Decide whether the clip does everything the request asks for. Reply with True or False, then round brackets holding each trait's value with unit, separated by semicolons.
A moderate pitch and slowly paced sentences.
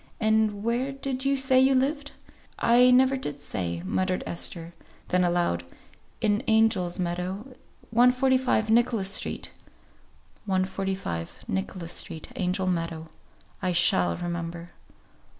False (195 Hz; 115 wpm)